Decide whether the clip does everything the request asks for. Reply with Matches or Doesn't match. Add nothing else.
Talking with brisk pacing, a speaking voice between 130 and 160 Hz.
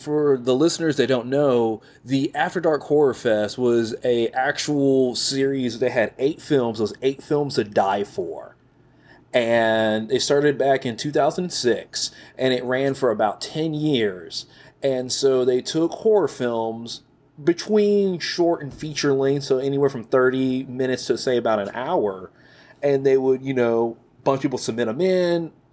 Doesn't match